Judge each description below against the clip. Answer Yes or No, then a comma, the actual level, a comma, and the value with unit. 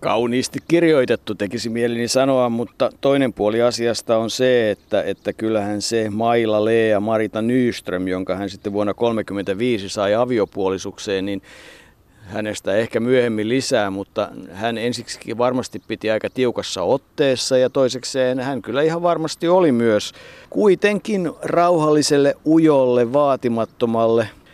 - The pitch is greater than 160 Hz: No, low, 115 Hz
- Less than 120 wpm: No, average, 125 wpm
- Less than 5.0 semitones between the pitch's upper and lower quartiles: Yes, average, 3.5 semitones